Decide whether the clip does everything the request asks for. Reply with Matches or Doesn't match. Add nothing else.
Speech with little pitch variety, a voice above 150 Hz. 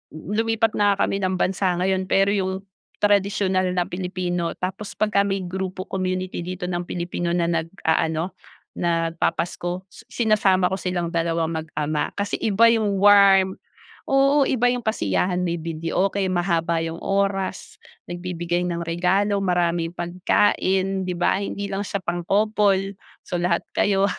Matches